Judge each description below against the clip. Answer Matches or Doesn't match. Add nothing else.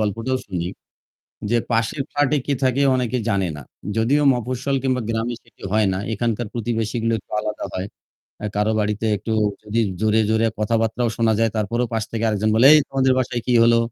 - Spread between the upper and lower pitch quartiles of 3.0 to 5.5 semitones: Doesn't match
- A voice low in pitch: Matches